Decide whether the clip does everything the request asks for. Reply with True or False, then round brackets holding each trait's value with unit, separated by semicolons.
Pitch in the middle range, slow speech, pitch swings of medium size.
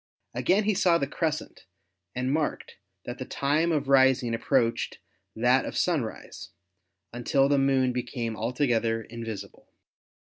False (130 Hz; 125 wpm; 3.8 semitones)